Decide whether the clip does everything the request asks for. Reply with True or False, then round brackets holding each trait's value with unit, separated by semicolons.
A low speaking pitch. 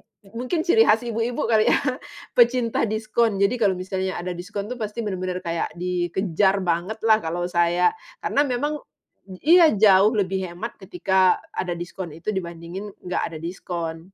False (195 Hz)